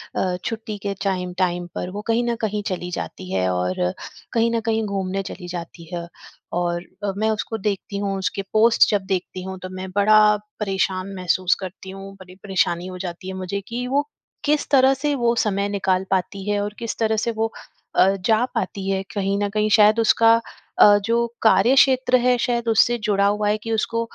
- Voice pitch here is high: Yes, high, 200 Hz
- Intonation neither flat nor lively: Yes, average, 3.3 semitones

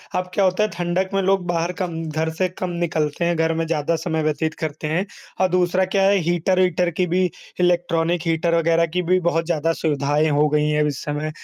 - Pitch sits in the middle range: Yes, medium, 170 Hz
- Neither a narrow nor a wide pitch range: No, narrow, 2.3 semitones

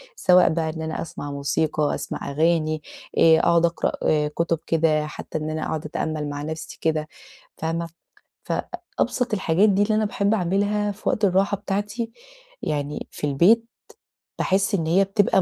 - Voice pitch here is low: No, medium, 170 Hz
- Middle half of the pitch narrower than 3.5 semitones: No, average, 4.3 semitones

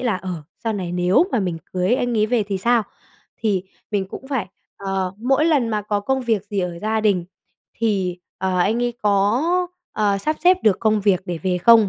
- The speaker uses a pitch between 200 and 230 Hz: Yes, high, 210 Hz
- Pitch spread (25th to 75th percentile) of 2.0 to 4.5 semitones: Yes, average, 3.7 semitones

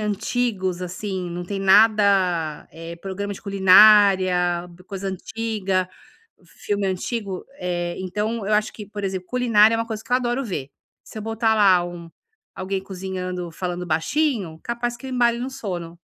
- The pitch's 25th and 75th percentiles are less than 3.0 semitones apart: No, average, 3.4 semitones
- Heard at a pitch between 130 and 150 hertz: No, high, 195 Hz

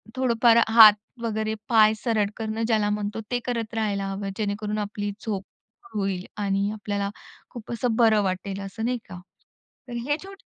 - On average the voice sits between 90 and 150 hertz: No, high, 215 Hz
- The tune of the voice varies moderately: No, narrow, 2.2 semitones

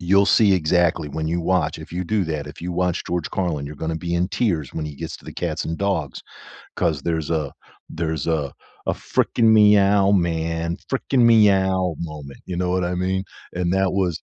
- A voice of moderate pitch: No, very low, 85 Hz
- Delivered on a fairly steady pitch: No, average, 3.0 semitones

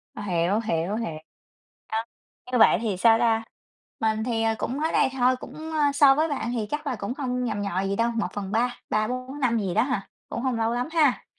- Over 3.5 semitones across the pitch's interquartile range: No, average, 3.2 semitones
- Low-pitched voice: No, high, 230 Hz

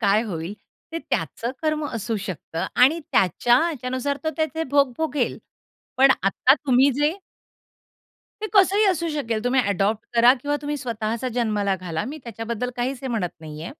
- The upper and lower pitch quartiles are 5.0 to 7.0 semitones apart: Yes, average, 5.3 semitones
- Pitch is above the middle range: Yes, high, 245 Hz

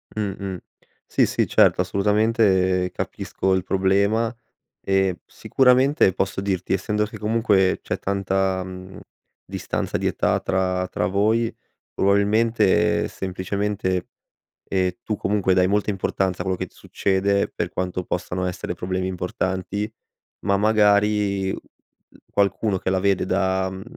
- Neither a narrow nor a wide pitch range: No, narrow, 1.9 semitones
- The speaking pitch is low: Yes, very low, 95 Hz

